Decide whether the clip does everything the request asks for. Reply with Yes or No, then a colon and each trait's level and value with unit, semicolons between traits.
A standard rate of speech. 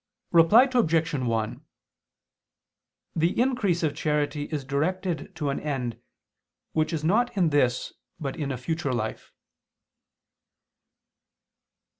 No: slow, 110 wpm